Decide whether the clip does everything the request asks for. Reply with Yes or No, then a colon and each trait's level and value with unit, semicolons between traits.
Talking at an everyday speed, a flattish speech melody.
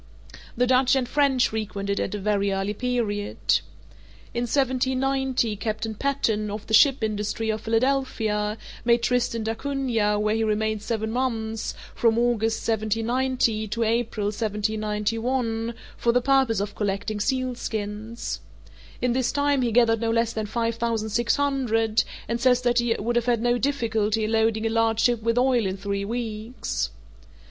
Yes: average, 155 wpm; narrow, 2.3 semitones